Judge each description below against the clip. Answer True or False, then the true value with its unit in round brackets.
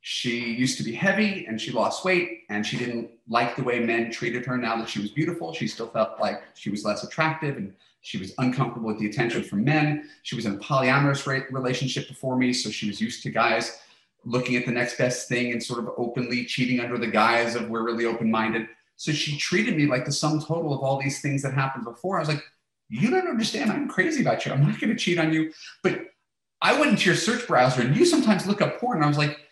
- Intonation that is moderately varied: True (4.6 semitones)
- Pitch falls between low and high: False (125 Hz)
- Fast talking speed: True (245 wpm)